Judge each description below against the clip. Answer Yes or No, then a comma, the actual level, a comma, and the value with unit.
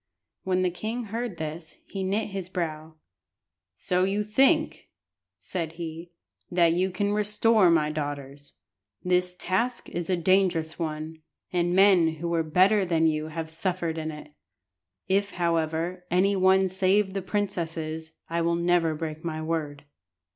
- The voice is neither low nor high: Yes, medium, 175 Hz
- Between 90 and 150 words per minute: Yes, average, 145 wpm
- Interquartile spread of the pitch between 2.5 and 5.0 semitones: Yes, average, 3.0 semitones